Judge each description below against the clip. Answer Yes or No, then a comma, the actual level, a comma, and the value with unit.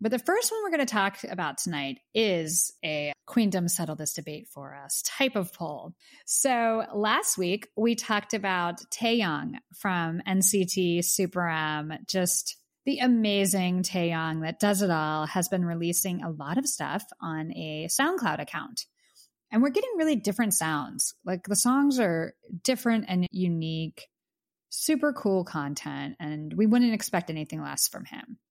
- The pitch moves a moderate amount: No, wide, 5.9 semitones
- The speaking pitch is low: No, high, 190 Hz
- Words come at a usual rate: Yes, average, 155 wpm